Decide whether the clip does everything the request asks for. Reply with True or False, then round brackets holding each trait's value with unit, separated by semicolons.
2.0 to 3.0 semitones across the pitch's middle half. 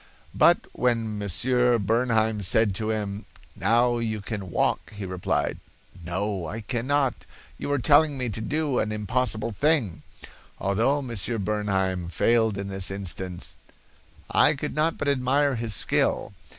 False (4.0 semitones)